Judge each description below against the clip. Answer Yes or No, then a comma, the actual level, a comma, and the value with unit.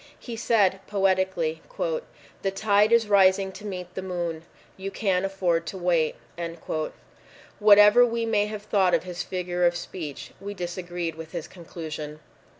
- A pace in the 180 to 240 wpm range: No, average, 150 wpm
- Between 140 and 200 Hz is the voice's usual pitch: Yes, high, 190 Hz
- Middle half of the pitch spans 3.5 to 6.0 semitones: No, average, 3.0 semitones